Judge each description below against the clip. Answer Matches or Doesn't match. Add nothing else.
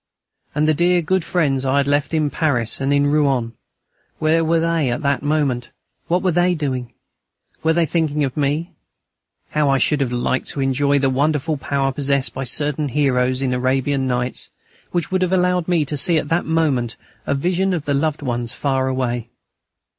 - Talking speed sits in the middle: Matches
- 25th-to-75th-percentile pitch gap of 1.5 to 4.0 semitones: Matches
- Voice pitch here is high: Doesn't match